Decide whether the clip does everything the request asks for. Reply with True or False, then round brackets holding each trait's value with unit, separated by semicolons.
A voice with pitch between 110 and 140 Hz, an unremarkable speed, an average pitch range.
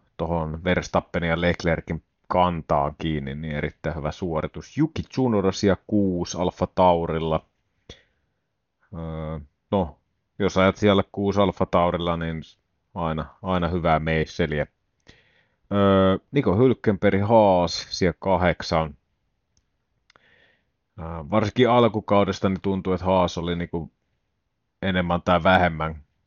False (90 Hz; 105 wpm; 3.1 semitones)